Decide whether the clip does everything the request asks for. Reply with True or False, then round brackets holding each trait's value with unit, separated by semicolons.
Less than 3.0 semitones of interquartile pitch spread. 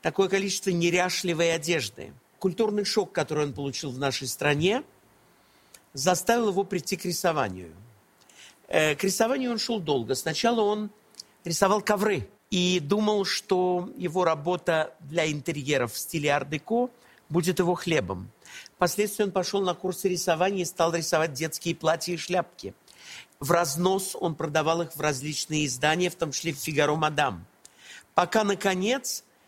False (3.9 semitones)